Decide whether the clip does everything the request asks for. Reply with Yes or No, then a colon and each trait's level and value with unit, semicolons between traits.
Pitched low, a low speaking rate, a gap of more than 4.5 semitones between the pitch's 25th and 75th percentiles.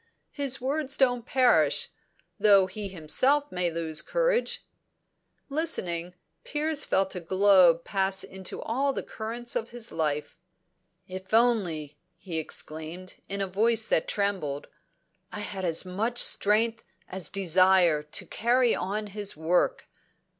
No: high, 195 Hz; slow, 130 wpm; average, 5.2 semitones